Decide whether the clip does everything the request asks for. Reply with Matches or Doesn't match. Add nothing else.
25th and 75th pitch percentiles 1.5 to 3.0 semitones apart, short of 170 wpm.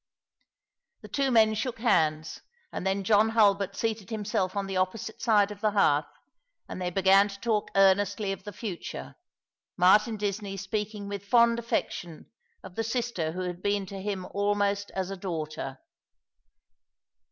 Matches